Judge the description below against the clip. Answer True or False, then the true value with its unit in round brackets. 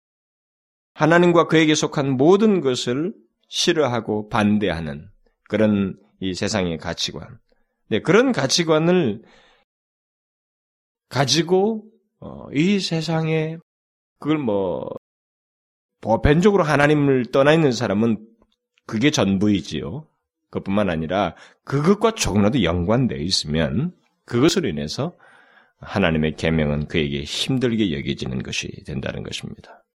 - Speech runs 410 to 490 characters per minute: False (250 characters per minute)